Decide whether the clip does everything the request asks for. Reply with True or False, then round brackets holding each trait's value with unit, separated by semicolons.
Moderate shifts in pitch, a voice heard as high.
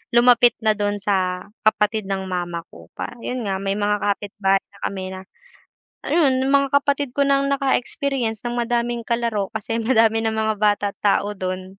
True (3.4 semitones; 220 Hz)